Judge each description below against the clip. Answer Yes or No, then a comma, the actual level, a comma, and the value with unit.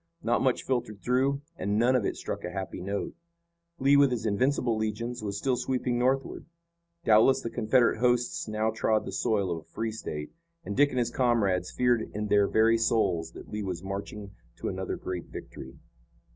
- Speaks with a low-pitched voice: Yes, low, 110 Hz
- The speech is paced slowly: No, average, 185 wpm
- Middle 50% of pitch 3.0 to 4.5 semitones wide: Yes, average, 3.5 semitones